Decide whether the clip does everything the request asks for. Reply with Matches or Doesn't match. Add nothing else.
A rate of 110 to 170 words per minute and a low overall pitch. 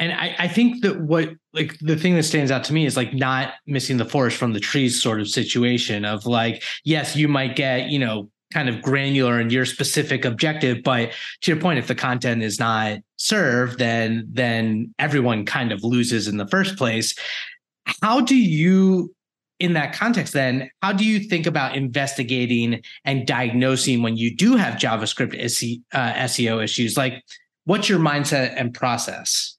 Doesn't match